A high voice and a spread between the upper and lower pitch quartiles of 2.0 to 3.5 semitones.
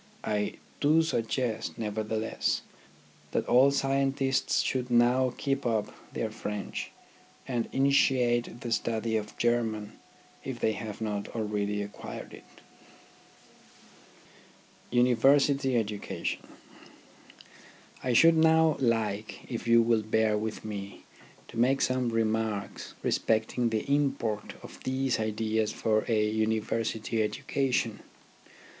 No: low, 115 Hz; average, 3.0 semitones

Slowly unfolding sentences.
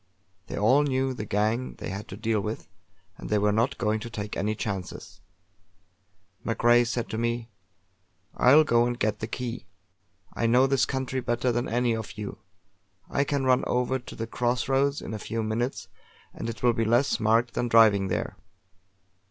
No: average, 185 wpm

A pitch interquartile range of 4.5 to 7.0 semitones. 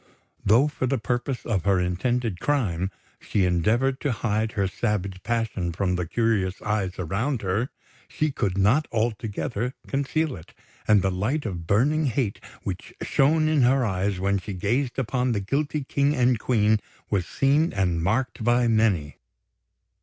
Yes: average, 5.2 semitones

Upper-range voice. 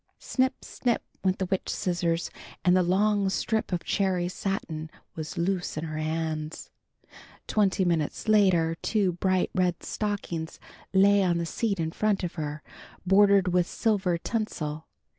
No: medium, 180 Hz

